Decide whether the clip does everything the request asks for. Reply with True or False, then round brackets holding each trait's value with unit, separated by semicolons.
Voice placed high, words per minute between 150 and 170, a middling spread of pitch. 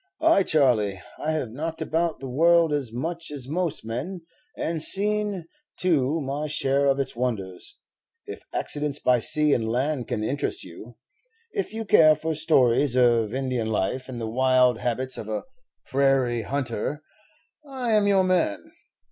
False (140 Hz; 155 wpm; 5.0 semitones)